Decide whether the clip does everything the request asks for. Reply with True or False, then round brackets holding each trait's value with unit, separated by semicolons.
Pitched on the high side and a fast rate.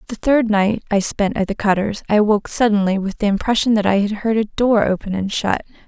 True (210 Hz; 235 wpm)